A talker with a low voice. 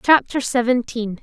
No: high, 245 Hz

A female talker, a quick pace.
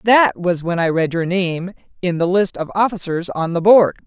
Yes: female; fast, 220 wpm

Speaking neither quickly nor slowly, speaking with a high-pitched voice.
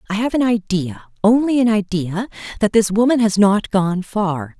Yes: average, 155 wpm; high, 210 Hz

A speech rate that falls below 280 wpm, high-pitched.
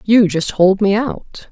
Yes: average, 200 wpm; high, 200 Hz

